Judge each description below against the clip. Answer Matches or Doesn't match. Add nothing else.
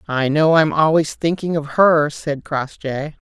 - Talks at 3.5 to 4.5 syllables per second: Matches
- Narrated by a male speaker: Doesn't match